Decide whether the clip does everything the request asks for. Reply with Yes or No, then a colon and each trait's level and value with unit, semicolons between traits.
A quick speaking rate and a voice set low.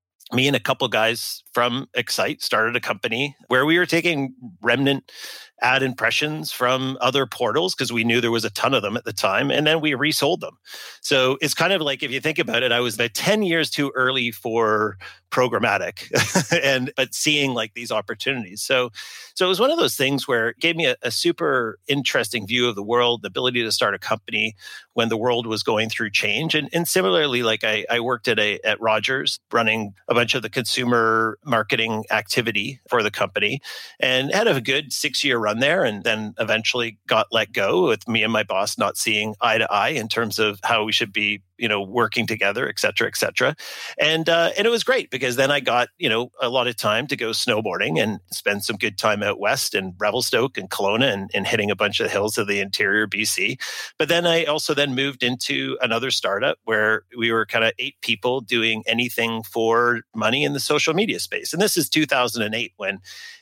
Yes: fast, 215 wpm; low, 120 Hz